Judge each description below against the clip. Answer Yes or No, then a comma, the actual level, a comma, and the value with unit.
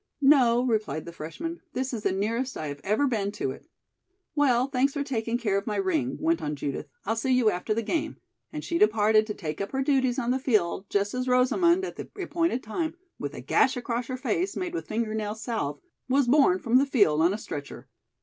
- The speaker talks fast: Yes, fast, 225 wpm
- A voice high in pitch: Yes, high, 240 Hz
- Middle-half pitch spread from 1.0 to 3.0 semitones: No, average, 4.8 semitones